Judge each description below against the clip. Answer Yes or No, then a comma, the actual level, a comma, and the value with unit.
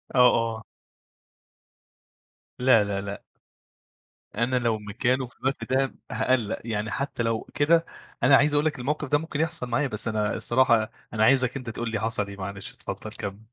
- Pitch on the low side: Yes, low, 120 Hz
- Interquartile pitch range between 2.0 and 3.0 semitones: No, average, 3.8 semitones